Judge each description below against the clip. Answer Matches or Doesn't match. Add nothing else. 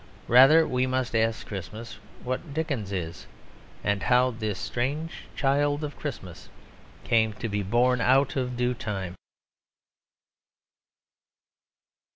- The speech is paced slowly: Matches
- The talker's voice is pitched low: Matches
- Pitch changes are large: Doesn't match